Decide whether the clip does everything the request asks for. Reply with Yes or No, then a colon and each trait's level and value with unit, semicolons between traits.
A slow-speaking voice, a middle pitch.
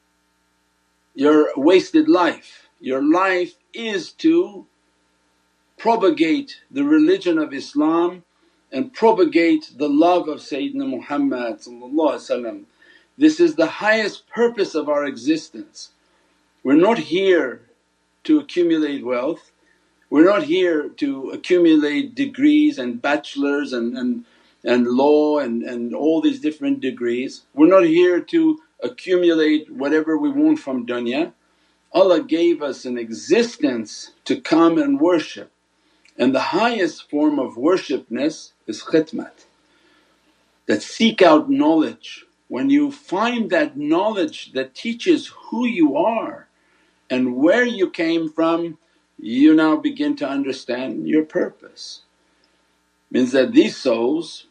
No: slow, 120 wpm; high, 245 Hz